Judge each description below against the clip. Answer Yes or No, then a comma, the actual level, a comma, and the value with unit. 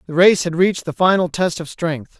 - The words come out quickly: Yes, fast, 245 wpm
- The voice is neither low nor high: Yes, medium, 170 Hz